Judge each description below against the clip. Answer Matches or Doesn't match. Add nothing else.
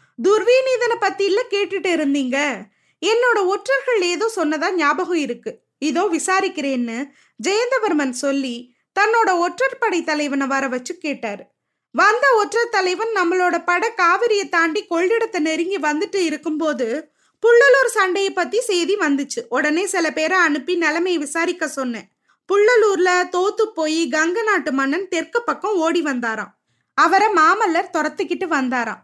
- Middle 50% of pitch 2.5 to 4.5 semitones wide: Doesn't match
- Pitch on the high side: Matches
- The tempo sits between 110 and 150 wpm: Matches